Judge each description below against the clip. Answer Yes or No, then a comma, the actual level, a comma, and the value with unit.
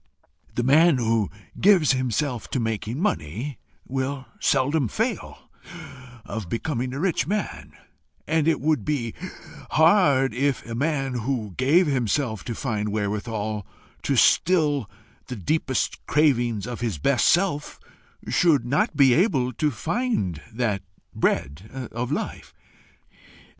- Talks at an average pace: No, slow, 125 wpm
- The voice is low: Yes, low, 130 Hz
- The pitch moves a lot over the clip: No, average, 5.0 semitones